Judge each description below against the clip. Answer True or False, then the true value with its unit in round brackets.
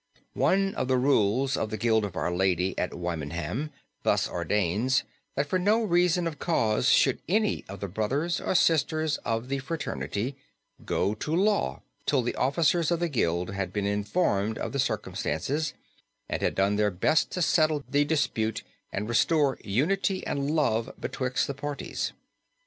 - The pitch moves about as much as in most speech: False (7.3 semitones)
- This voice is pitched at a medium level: False (130 Hz)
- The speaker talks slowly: False (165 wpm)